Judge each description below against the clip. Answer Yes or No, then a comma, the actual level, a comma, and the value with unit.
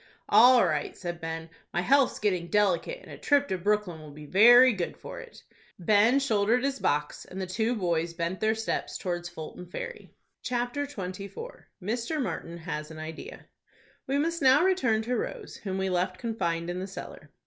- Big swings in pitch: Yes, wide, 6.1 semitones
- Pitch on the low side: No, high, 200 Hz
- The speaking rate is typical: Yes, average, 180 wpm